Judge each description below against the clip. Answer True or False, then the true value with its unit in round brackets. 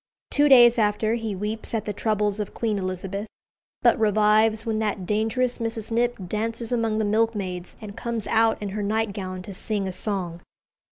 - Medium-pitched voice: False (215 Hz)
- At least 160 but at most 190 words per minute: True (175 wpm)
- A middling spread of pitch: False (2.0 semitones)